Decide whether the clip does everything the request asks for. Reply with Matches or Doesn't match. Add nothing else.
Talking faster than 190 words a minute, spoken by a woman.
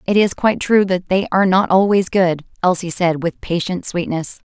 Matches